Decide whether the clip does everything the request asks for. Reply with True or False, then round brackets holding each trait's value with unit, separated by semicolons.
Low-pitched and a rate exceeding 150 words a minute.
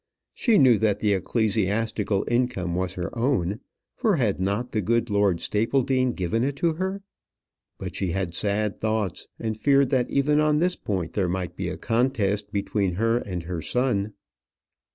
True (110 Hz; 170 wpm)